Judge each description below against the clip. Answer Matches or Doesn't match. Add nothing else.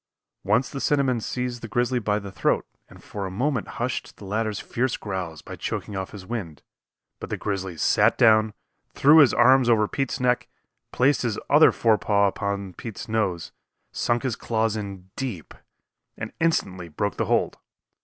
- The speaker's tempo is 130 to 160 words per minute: Doesn't match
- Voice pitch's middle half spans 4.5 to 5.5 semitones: Doesn't match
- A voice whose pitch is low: Matches